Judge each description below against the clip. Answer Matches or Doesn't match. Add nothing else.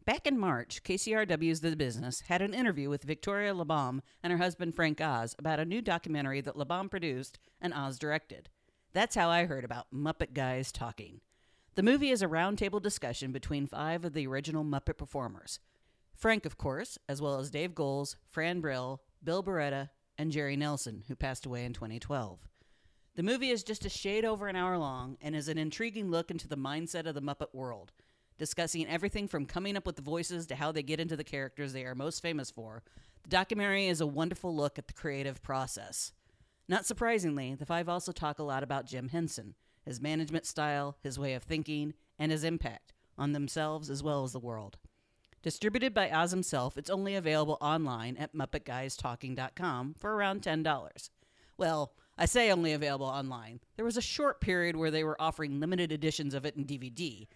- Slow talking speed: Doesn't match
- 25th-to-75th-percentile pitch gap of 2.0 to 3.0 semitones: Doesn't match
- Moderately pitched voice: Matches